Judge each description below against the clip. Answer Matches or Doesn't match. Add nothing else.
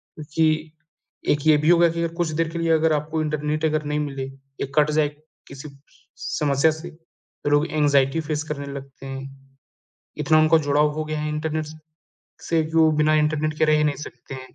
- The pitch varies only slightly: Matches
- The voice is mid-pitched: Matches